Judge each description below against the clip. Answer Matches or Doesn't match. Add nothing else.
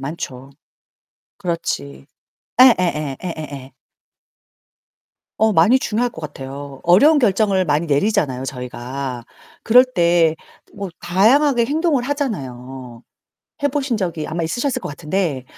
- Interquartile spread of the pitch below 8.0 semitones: Doesn't match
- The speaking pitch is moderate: Matches